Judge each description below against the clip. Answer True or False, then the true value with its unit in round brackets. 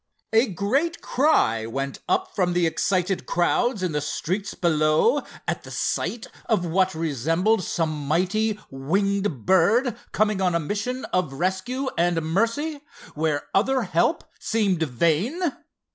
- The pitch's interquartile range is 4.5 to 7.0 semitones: True (5.6 semitones)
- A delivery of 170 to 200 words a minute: False (135 wpm)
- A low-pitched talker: False (185 Hz)